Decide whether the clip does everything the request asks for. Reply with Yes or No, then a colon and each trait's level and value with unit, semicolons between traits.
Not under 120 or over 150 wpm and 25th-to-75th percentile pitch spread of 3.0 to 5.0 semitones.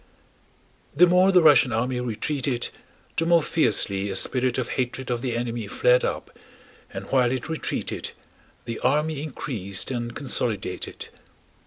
Yes: average, 140 wpm; average, 4.4 semitones